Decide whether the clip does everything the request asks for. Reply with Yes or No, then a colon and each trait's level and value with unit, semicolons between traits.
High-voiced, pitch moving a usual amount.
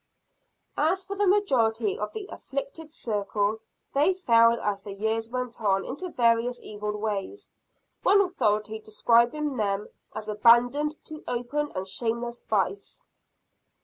No: high, 235 Hz; wide, 6.1 semitones